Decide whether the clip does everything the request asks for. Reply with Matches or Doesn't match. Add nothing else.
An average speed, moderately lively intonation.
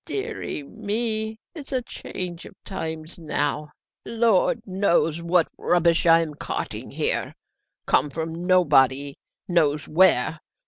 Doesn't match